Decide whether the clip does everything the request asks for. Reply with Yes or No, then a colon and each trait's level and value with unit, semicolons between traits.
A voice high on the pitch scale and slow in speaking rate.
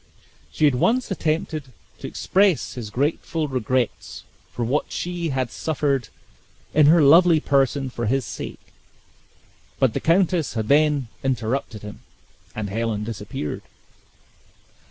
No: low, 135 Hz; slow, 125 wpm